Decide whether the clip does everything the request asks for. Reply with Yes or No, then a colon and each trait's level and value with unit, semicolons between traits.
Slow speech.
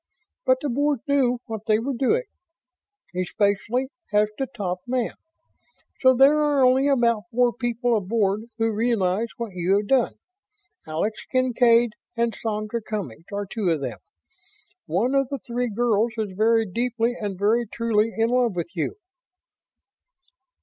No: average, 150 wpm